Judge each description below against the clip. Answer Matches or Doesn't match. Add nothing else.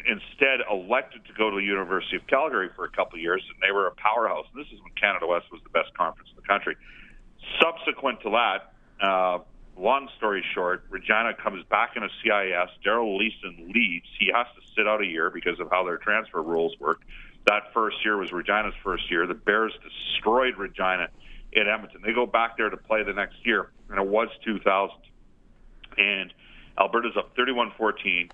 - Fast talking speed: Doesn't match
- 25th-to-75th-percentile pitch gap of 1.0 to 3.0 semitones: Doesn't match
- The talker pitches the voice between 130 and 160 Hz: Doesn't match